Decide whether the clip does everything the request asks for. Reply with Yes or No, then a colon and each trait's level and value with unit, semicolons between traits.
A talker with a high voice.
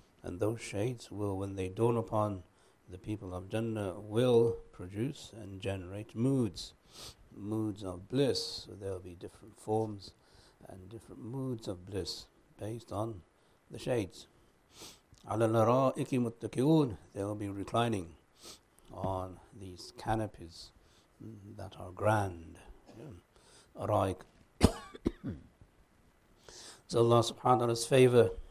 No: low, 105 Hz